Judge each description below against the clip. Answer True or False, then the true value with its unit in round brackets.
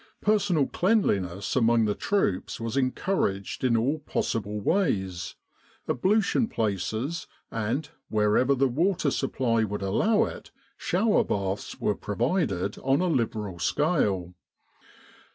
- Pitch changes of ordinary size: False (8.2 semitones)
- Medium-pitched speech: False (115 Hz)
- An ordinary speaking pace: False (115 wpm)